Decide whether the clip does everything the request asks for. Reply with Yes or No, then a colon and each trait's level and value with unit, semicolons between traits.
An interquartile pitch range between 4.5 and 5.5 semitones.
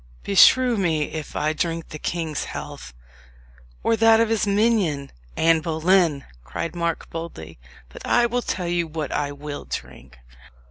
Yes: average, 4.8 semitones